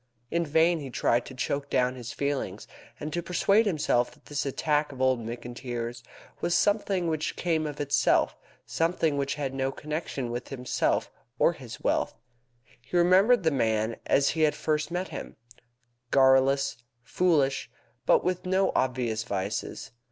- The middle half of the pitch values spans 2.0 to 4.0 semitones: No, average, 4.8 semitones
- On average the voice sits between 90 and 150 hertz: Yes, medium, 140 Hz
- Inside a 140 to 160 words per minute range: Yes, average, 155 wpm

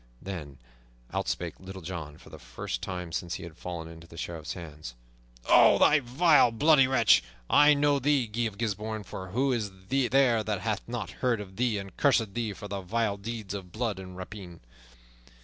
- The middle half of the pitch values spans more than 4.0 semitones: Yes, average, 5.1 semitones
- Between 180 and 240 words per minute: Yes, average, 190 wpm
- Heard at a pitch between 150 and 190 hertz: No, low, 105 Hz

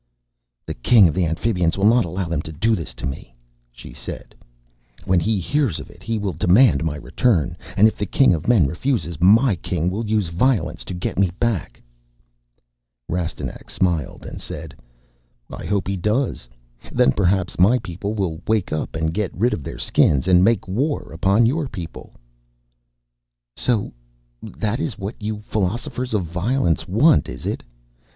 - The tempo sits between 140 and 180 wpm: Yes, average, 170 wpm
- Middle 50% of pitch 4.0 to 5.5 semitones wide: Yes, average, 5.2 semitones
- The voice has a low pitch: Yes, very low, 95 Hz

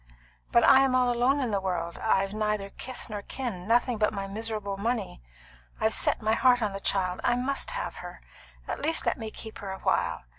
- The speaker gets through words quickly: Yes, fast, 210 wpm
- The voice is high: Yes, high, 220 Hz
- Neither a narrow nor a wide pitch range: Yes, average, 3.9 semitones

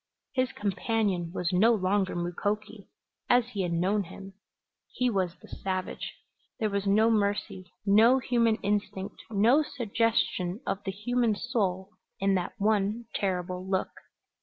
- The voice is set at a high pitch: Yes, high, 200 Hz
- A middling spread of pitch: Yes, average, 3.1 semitones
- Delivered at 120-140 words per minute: Yes, slow, 135 wpm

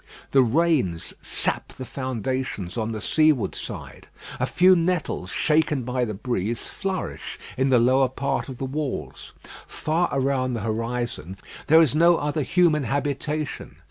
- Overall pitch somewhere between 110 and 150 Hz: Yes, low, 135 Hz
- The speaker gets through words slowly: No, average, 145 wpm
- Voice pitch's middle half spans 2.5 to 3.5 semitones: No, average, 4.3 semitones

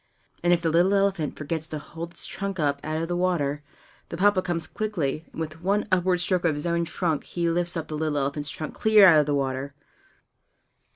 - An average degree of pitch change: Yes, average, 3.1 semitones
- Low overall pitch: No, medium, 165 Hz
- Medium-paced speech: No, fast, 220 wpm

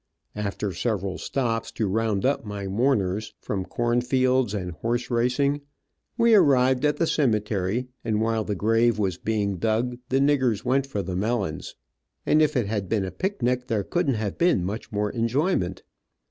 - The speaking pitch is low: Yes, low, 115 Hz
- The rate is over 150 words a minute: Yes, average, 170 wpm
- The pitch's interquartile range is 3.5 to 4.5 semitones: Yes, average, 4.1 semitones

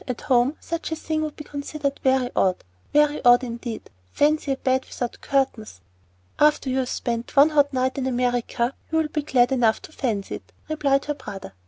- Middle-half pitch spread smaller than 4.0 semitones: Yes, average, 3.3 semitones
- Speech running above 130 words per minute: Yes, average, 185 wpm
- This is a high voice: Yes, very high, 265 Hz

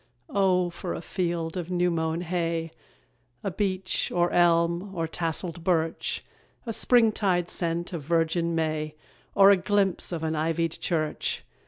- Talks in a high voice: No, medium, 170 Hz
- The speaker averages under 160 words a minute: Yes, average, 145 wpm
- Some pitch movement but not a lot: No, narrow, 1.9 semitones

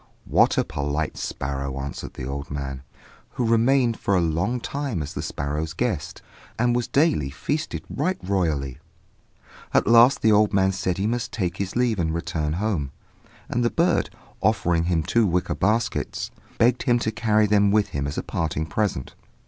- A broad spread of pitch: Yes, wide, 7.1 semitones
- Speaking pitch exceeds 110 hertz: No, very low, 95 Hz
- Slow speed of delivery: No, average, 180 wpm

